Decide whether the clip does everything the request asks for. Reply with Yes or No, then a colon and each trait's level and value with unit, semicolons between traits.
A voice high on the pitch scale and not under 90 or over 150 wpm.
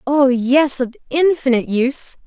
Yes: very high, 265 Hz; slow, 135 wpm